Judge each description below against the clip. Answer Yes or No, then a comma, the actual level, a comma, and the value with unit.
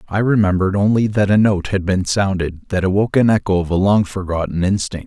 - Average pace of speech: No, fast, 215 wpm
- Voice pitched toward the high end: No, very low, 95 Hz